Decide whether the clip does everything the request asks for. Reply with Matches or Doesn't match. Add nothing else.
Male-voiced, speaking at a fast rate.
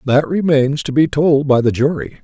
Matches